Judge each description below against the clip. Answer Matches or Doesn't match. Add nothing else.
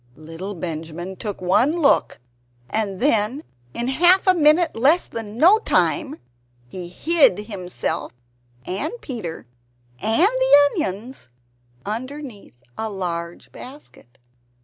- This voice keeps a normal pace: Doesn't match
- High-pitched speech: Matches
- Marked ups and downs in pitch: Matches